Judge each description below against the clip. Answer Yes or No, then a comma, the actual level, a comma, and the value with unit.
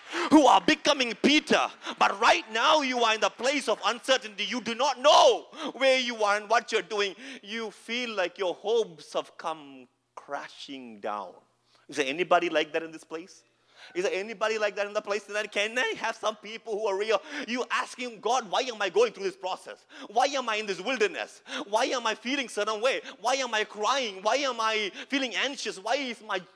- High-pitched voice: Yes, high, 225 Hz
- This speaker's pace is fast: Yes, fast, 215 wpm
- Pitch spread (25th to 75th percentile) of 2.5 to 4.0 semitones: No, average, 4.5 semitones